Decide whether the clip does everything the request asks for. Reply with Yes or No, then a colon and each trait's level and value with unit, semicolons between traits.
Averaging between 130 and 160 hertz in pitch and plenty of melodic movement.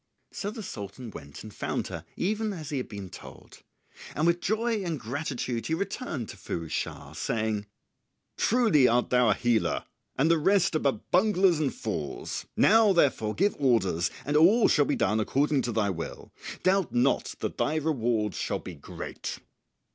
Yes: medium, 140 Hz; wide, 8.5 semitones